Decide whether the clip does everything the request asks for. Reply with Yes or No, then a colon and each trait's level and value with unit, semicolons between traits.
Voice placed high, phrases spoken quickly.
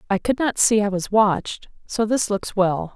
Yes: high, 210 Hz; fast, 225 wpm